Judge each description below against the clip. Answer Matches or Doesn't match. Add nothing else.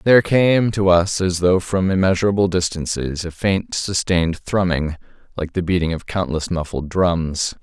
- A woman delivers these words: Doesn't match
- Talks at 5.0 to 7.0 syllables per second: Doesn't match